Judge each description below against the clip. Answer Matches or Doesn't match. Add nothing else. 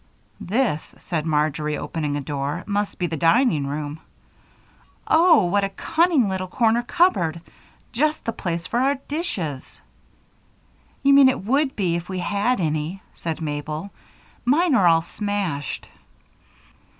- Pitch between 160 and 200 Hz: Matches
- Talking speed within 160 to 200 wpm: Doesn't match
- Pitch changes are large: Matches